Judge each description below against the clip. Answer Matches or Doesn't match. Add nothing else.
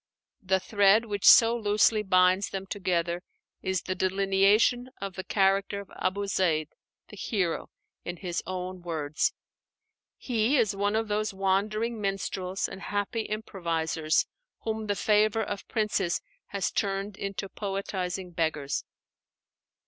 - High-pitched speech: Matches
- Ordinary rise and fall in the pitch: Doesn't match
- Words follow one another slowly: Matches